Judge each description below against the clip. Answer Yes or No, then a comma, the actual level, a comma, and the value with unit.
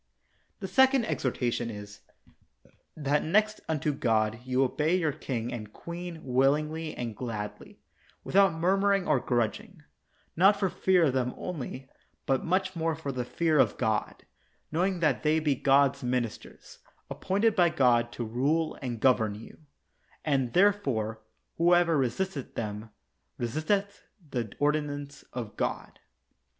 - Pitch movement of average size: No, wide, 5.9 semitones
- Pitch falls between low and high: Yes, medium, 145 Hz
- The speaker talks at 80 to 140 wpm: Yes, slow, 135 wpm